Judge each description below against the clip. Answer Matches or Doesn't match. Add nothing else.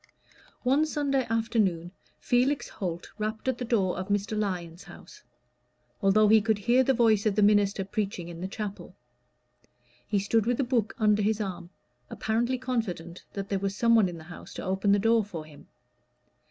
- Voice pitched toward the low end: Doesn't match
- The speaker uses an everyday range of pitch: Matches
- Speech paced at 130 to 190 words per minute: Matches